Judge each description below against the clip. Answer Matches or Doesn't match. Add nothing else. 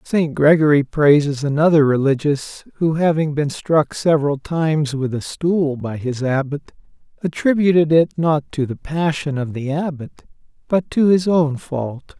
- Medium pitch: Matches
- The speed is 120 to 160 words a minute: Matches